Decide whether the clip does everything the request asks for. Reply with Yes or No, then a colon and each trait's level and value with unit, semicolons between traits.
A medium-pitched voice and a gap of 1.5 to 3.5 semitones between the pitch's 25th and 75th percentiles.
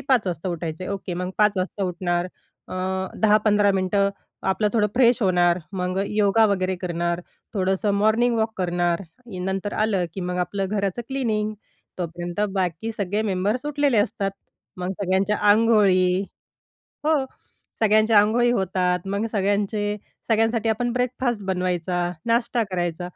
No: high, 200 Hz; average, 3.2 semitones